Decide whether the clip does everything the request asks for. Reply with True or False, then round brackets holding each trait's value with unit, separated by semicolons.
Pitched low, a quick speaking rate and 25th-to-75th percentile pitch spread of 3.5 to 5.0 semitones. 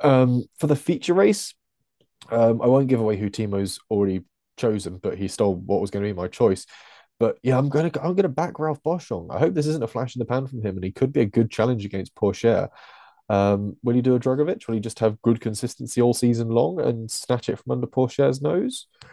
True (120 Hz; 240 wpm; 4.6 semitones)